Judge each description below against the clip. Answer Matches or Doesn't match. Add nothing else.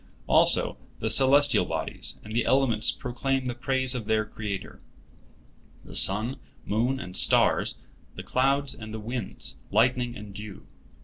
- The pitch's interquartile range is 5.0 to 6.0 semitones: Doesn't match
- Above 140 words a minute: Doesn't match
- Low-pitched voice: Matches